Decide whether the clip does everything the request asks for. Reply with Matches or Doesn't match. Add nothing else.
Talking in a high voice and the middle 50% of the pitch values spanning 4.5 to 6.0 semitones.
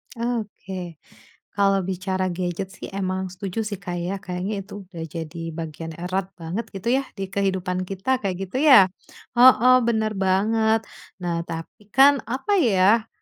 Doesn't match